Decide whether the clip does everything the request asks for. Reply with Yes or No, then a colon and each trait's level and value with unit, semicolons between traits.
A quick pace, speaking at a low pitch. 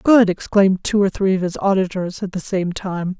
No: fast, 225 wpm; high, 190 Hz